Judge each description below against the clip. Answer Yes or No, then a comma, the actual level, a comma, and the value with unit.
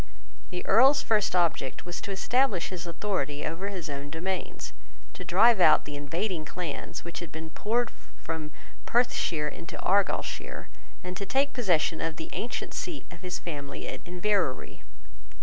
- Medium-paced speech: Yes, average, 155 wpm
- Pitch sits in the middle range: Yes, medium, 180 Hz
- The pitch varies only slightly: No, average, 4.3 semitones